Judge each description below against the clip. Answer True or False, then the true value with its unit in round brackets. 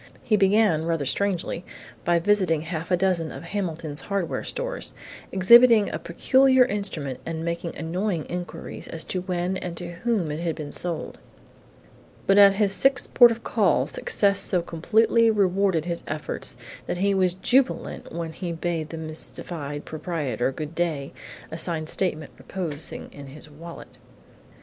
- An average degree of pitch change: True (3.8 semitones)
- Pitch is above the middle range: False (175 Hz)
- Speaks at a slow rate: False (155 wpm)